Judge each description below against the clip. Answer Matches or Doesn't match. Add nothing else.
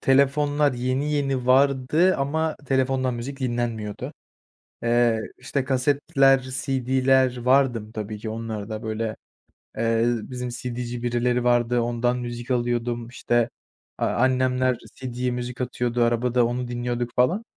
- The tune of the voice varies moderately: Doesn't match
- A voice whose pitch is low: Matches